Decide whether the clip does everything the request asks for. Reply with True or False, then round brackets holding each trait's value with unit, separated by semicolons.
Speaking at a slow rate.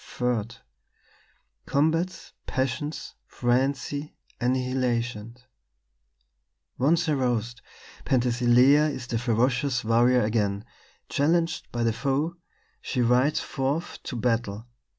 True (90 wpm)